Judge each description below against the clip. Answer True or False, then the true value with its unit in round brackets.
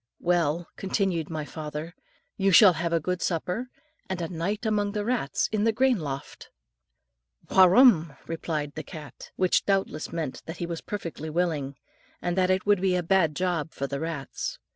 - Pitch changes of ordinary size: True (3.6 semitones)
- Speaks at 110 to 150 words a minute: False (175 wpm)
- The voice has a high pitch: False (175 Hz)